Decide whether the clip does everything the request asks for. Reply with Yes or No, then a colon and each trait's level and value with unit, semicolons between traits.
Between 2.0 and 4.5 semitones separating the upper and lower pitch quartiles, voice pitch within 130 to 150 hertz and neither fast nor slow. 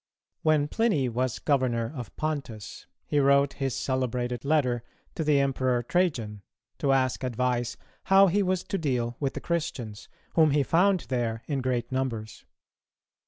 Yes: average, 3.9 semitones; low, 135 Hz; average, 150 wpm